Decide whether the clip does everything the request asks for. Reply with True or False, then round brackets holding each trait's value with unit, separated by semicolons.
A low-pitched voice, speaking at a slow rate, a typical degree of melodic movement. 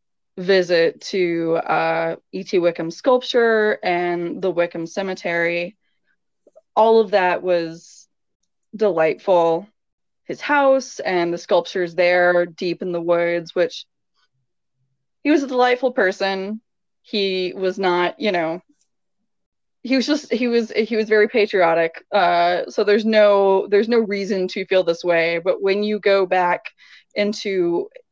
False (185 Hz; 130 wpm; 3.7 semitones)